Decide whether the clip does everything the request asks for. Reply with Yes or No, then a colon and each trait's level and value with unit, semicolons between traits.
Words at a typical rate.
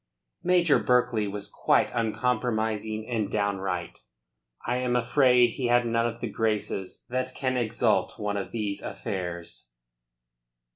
No: slow, 130 wpm